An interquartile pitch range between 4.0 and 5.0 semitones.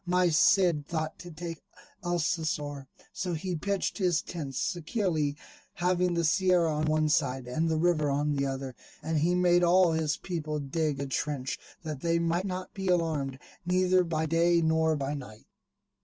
No: average, 2.9 semitones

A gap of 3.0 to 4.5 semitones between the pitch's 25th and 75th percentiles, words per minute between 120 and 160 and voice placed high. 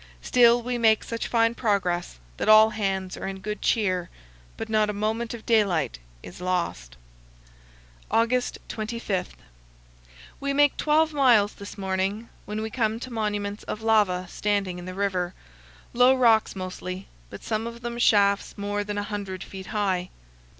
Yes: average, 3.3 semitones; average, 155 wpm; high, 210 Hz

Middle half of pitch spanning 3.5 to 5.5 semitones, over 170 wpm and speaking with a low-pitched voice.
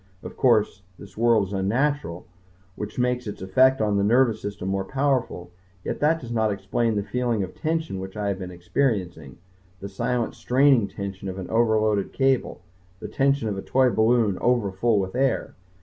Yes: average, 4.3 semitones; average, 180 wpm; low, 110 Hz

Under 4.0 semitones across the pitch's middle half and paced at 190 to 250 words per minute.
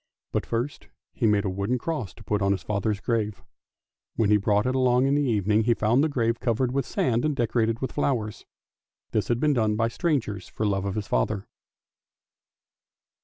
Yes: average, 3.4 semitones; average, 200 wpm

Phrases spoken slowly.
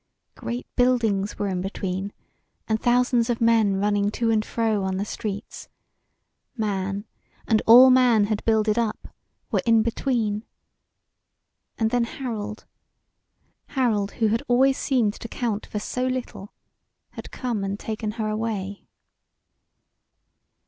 Yes: slow, 130 wpm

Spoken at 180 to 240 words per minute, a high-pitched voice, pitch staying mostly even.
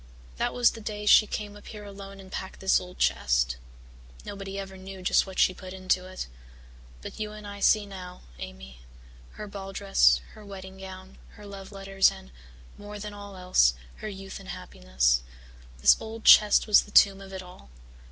Yes: average, 190 wpm; high, 195 Hz; narrow, 1.7 semitones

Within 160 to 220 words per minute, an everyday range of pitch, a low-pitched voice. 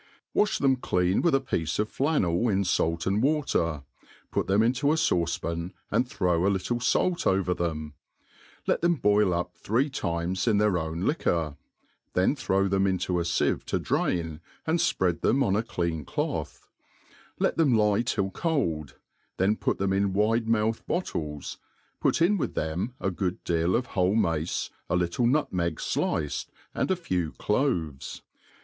No: average, 170 wpm; wide, 6.2 semitones; very low, 95 Hz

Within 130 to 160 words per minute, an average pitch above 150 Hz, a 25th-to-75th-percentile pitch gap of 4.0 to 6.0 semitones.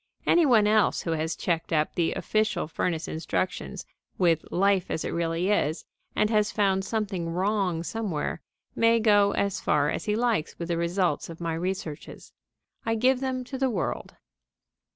No: average, 170 wpm; high, 190 Hz; average, 4.4 semitones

